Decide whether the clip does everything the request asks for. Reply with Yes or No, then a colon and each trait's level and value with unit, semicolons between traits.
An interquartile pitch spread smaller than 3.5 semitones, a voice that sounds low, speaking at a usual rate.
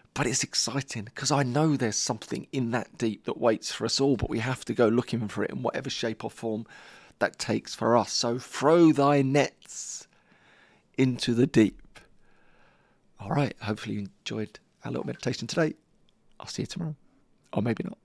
No: average, 3.8 semitones; low, 120 Hz; average, 185 wpm